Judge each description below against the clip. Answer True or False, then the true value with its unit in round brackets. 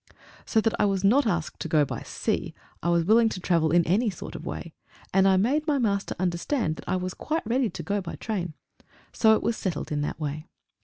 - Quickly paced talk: True (235 wpm)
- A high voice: True (195 Hz)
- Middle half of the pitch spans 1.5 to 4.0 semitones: False (4.7 semitones)